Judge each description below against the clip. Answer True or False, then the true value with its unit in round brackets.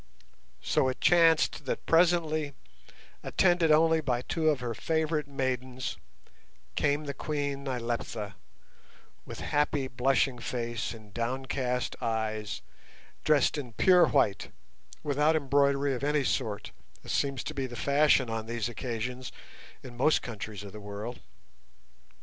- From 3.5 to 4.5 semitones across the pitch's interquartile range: True (4.0 semitones)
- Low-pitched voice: True (130 Hz)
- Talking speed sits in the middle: False (130 wpm)